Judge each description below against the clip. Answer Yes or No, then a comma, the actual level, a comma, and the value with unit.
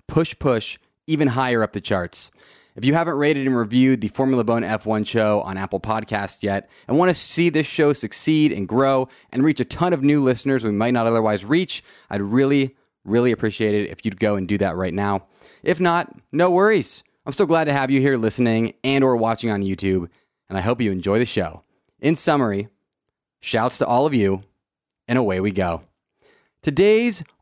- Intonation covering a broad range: Yes, wide, 5.7 semitones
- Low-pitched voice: Yes, low, 115 Hz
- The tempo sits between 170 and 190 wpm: No, average, 200 wpm